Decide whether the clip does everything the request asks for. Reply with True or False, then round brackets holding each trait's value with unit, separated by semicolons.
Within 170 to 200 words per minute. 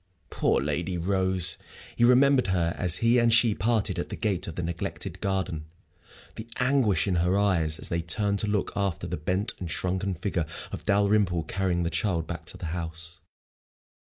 True (180 wpm)